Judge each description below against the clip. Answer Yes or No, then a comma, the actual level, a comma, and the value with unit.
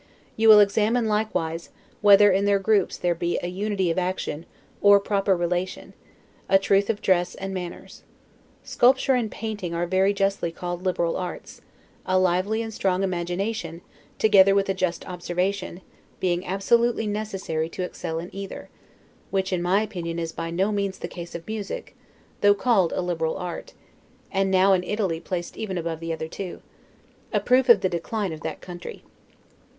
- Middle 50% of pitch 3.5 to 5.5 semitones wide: No, average, 2.7 semitones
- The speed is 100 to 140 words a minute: No, average, 170 wpm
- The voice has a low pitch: No, high, 190 Hz